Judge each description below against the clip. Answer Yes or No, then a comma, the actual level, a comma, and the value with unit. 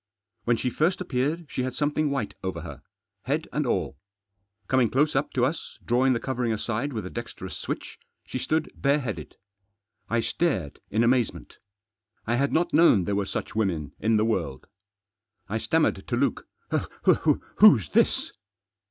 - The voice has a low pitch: Yes, low, 120 Hz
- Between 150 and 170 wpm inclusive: Yes, average, 160 wpm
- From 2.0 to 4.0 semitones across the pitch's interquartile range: No, average, 4.8 semitones